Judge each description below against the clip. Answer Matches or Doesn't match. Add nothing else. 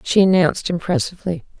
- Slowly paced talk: Matches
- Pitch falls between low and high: Matches